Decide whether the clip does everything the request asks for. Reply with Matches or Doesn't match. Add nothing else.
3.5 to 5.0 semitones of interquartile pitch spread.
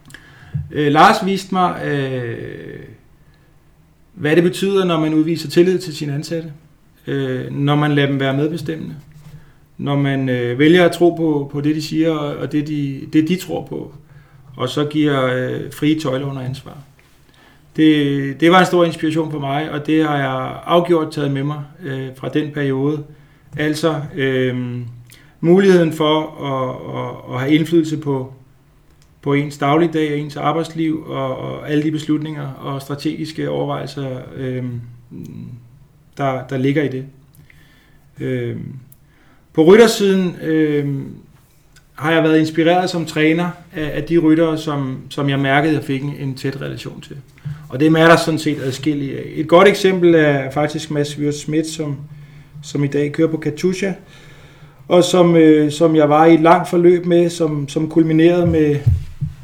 Doesn't match